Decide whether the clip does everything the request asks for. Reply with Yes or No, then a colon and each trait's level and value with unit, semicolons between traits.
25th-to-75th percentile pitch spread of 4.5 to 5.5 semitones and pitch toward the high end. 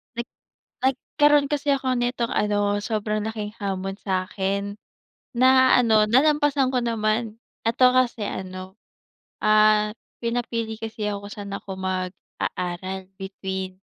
No: average, 3.8 semitones; high, 215 Hz